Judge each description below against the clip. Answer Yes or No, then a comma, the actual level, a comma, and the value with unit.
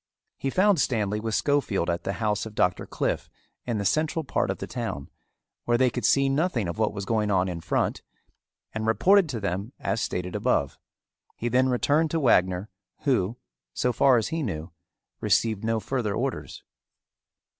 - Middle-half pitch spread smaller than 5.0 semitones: No, wide, 5.4 semitones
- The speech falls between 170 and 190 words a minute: Yes, average, 175 wpm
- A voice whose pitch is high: No, low, 110 Hz